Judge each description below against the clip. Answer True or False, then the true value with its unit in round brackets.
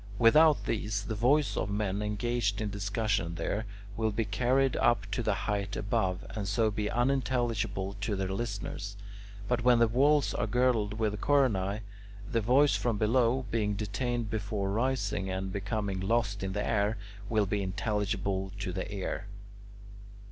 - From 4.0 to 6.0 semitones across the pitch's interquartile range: False (2.9 semitones)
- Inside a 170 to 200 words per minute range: False (155 wpm)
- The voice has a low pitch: True (105 Hz)